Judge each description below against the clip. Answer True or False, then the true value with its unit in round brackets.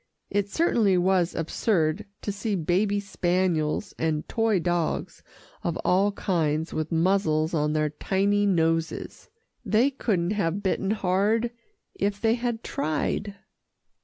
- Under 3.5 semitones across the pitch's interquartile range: False (3.8 semitones)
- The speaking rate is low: True (125 wpm)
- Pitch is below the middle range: False (190 Hz)